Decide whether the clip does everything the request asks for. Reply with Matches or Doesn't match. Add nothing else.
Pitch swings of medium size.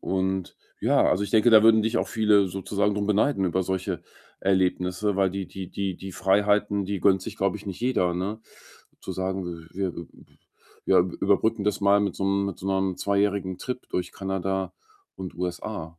Doesn't match